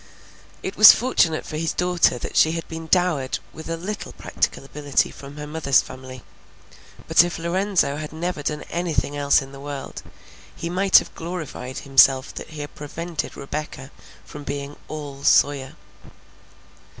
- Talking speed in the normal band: Yes, average, 160 wpm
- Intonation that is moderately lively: Yes, average, 3.3 semitones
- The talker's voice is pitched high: No, medium, 150 Hz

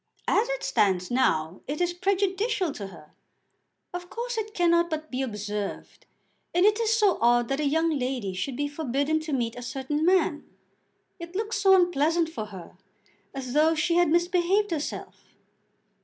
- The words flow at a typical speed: Yes, average, 170 wpm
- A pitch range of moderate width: No, wide, 6.3 semitones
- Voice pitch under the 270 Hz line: No, very high, 315 Hz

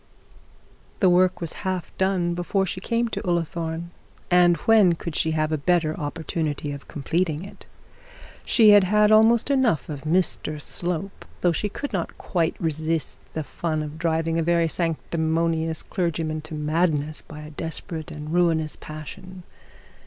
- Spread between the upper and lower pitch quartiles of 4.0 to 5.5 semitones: No, average, 2.7 semitones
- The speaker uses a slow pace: No, average, 155 wpm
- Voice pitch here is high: No, medium, 165 Hz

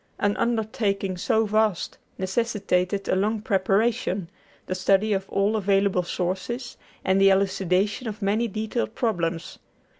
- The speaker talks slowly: Yes, slow, 125 wpm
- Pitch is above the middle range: Yes, high, 200 Hz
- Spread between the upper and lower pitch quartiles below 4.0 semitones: Yes, narrow, 2.6 semitones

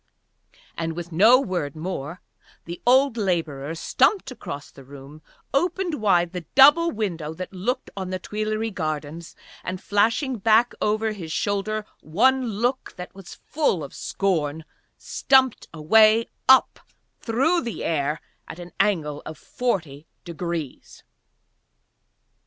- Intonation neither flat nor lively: No, wide, 6.1 semitones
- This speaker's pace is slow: Yes, slow, 130 wpm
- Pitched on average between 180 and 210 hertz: Yes, high, 190 Hz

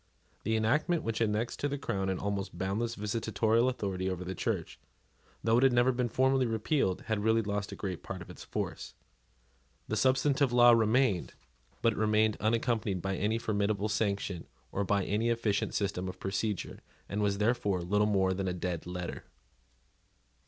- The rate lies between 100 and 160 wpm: No, average, 175 wpm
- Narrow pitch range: No, average, 3.2 semitones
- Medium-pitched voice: No, low, 105 Hz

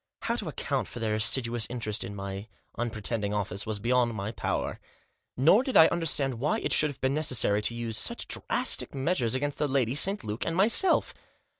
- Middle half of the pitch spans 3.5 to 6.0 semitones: Yes, average, 5.1 semitones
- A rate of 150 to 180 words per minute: No, average, 195 wpm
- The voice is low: Yes, low, 120 Hz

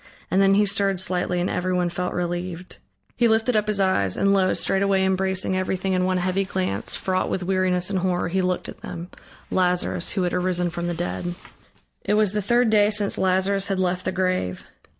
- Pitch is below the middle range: No, medium, 185 Hz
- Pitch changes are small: Yes, narrow, 1.6 semitones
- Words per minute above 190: Yes, average, 200 wpm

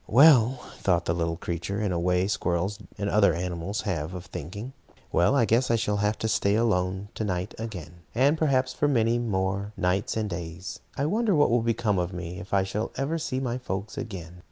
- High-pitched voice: No, low, 100 Hz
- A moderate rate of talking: No, fast, 210 wpm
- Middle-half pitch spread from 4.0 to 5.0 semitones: Yes, average, 4.5 semitones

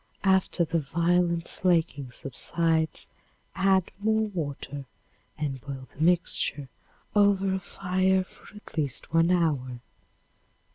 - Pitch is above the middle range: No, medium, 170 Hz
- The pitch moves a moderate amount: Yes, average, 4.6 semitones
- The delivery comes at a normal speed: No, slow, 110 wpm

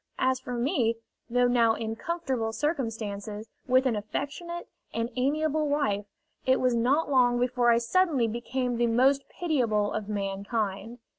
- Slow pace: No, average, 145 wpm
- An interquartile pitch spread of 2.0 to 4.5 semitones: Yes, average, 3.5 semitones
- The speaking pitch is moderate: No, high, 245 Hz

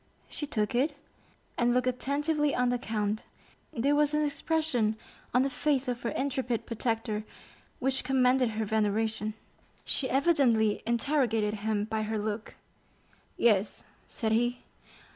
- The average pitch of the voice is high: Yes, high, 240 Hz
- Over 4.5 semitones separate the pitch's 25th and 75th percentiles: No, average, 3.8 semitones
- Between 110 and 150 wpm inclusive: Yes, slow, 135 wpm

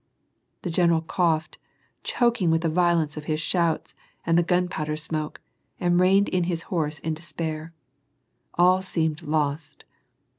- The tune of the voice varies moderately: No, narrow, 2.2 semitones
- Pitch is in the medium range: Yes, medium, 165 Hz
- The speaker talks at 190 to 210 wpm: No, average, 140 wpm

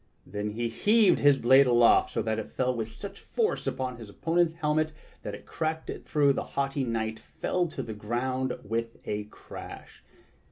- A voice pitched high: No, low, 130 Hz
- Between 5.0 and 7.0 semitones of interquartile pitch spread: Yes, wide, 5.4 semitones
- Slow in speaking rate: No, average, 190 wpm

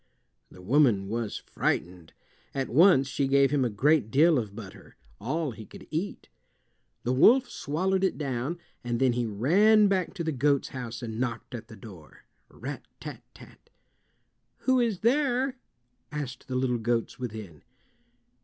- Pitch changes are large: Yes, wide, 6.6 semitones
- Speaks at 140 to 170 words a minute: Yes, average, 150 wpm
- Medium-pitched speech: No, low, 130 Hz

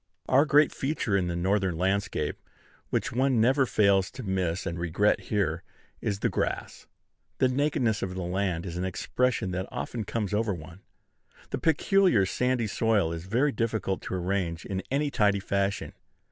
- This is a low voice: Yes, low, 100 Hz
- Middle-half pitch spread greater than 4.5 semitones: Yes, average, 5.1 semitones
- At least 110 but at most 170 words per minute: Yes, average, 165 wpm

